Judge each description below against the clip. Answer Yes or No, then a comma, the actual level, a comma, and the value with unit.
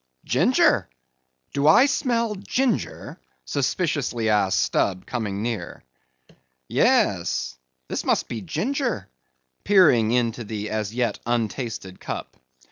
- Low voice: Yes, low, 120 Hz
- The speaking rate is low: Yes, slow, 105 wpm